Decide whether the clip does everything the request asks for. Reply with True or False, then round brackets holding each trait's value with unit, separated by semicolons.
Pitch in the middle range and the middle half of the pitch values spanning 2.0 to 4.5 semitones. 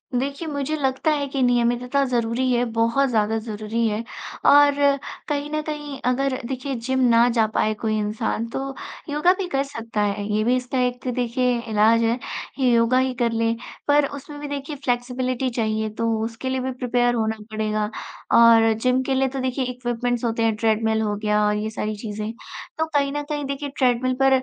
False (245 Hz; 3.1 semitones)